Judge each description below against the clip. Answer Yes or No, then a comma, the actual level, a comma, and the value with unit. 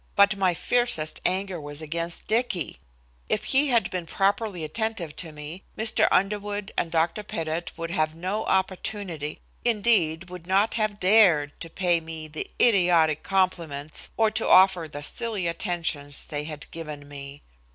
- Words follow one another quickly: No, average, 155 wpm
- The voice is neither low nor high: Yes, medium, 175 Hz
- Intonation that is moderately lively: Yes, average, 4.4 semitones